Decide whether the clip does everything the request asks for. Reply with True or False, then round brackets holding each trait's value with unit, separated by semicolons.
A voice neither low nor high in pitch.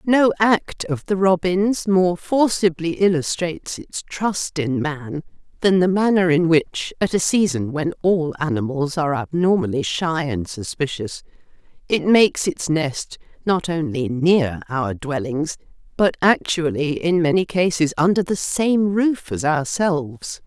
True (165 Hz)